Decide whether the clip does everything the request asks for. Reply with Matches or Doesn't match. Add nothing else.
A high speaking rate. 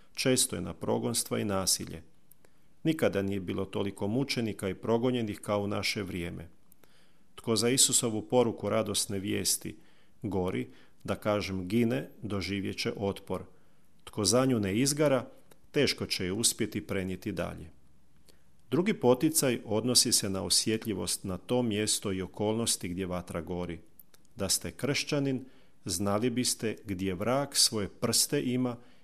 Doesn't match